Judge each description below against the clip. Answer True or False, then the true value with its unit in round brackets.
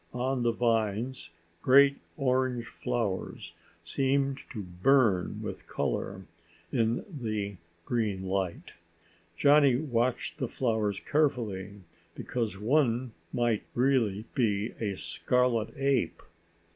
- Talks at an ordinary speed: False (100 wpm)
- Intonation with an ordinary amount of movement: True (4.0 semitones)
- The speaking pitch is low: True (120 Hz)